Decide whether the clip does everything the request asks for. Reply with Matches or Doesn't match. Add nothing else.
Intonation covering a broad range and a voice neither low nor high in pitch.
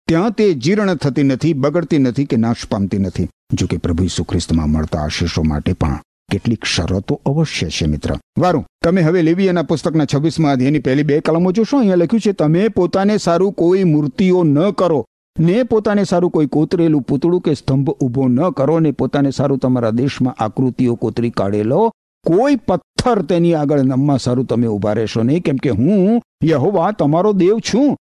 Matches